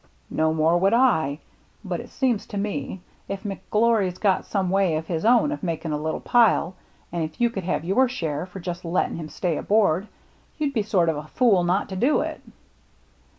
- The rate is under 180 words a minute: No, fast, 205 wpm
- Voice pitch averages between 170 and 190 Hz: Yes, medium, 185 Hz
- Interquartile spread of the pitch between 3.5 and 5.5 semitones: Yes, average, 4.9 semitones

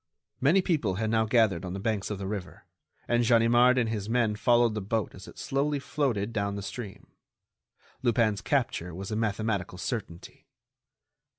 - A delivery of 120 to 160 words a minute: No, average, 170 wpm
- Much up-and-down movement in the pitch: No, average, 3.1 semitones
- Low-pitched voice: Yes, low, 110 Hz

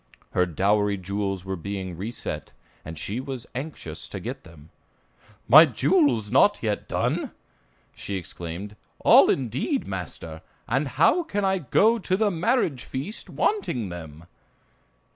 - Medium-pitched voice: No, low, 115 Hz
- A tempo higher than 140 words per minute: No, slow, 135 wpm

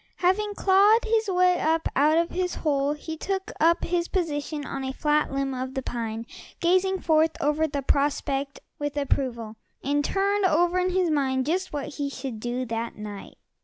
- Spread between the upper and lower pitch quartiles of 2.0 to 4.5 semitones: No, average, 5.0 semitones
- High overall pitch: Yes, very high, 300 Hz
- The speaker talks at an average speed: Yes, average, 180 wpm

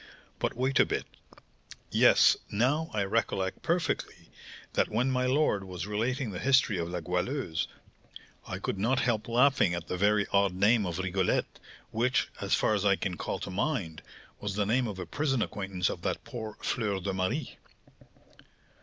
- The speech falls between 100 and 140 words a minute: No, average, 170 wpm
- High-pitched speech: No, low, 105 Hz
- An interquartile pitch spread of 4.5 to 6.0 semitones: Yes, average, 5.1 semitones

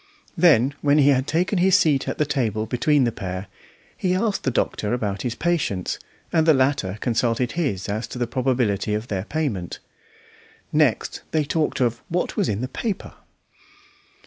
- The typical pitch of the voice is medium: No, low, 130 Hz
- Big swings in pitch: Yes, wide, 6.1 semitones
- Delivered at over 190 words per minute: No, average, 170 wpm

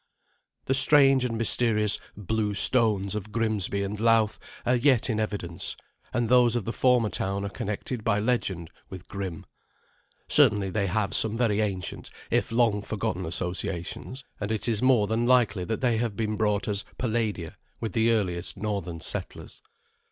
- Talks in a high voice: No, low, 110 Hz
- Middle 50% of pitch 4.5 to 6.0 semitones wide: No, average, 2.9 semitones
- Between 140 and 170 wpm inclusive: Yes, average, 160 wpm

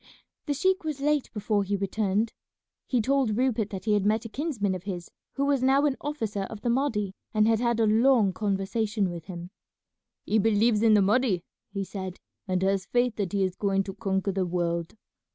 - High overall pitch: Yes, high, 210 Hz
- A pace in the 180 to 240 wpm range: Yes, fast, 205 wpm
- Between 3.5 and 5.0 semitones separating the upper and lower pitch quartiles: Yes, average, 3.8 semitones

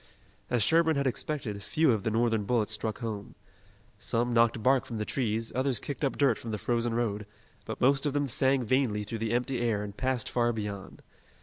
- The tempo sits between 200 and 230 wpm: Yes, fast, 205 wpm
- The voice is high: No, low, 120 Hz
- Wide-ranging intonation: No, average, 3.4 semitones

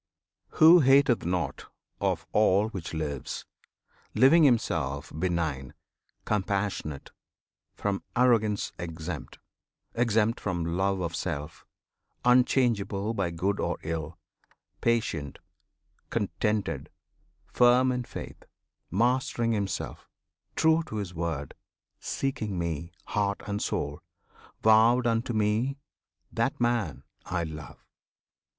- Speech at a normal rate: No, slow, 100 wpm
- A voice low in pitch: Yes, low, 100 Hz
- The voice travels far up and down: Yes, wide, 5.9 semitones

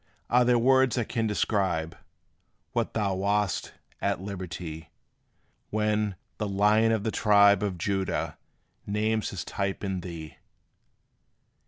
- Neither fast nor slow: No, slow, 125 wpm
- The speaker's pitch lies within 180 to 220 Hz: No, low, 100 Hz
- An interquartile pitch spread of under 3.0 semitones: Yes, narrow, 2.5 semitones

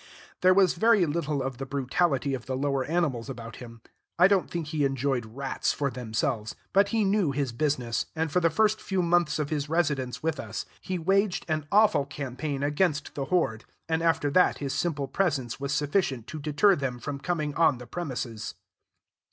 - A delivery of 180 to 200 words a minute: Yes, average, 190 wpm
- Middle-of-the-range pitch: Yes, medium, 145 Hz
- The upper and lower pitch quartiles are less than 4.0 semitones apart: No, average, 4.6 semitones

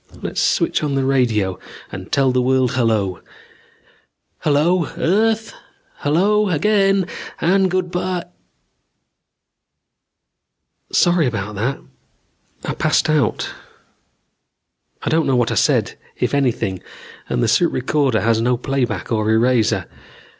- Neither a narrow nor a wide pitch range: No, wide, 7.1 semitones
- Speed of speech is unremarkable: No, slow, 120 wpm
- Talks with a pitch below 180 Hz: Yes, low, 135 Hz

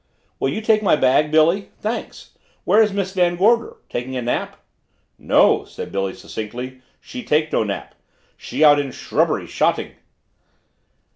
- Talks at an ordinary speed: Yes, average, 150 wpm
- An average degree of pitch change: No, wide, 7.8 semitones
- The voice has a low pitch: No, medium, 155 Hz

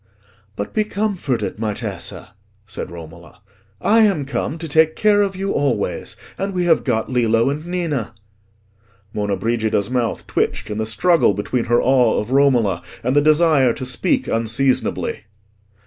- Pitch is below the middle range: Yes, low, 125 Hz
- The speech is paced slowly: No, average, 155 wpm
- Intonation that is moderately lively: No, wide, 6.6 semitones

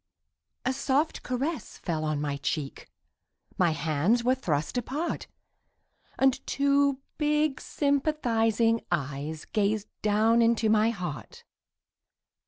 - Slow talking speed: Yes, slow, 105 wpm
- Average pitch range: No, wide, 8.7 semitones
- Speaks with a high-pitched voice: Yes, high, 225 Hz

